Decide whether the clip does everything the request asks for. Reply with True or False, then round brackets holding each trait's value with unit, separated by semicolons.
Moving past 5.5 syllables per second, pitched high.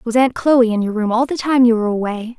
True (6.0 syllables/s; 235 Hz)